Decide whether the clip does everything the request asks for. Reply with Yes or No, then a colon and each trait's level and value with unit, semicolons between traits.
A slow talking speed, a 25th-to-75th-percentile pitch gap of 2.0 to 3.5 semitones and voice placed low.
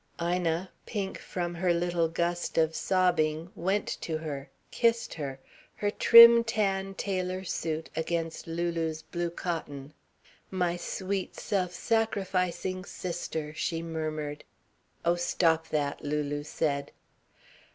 No: slow, 115 wpm; average, 2.7 semitones; medium, 170 Hz